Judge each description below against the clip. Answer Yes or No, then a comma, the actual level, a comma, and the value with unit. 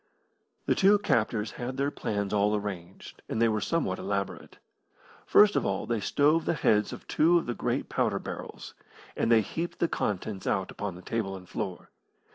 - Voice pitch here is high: No, low, 110 Hz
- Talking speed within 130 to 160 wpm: No, average, 185 wpm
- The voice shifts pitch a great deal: Yes, wide, 6.2 semitones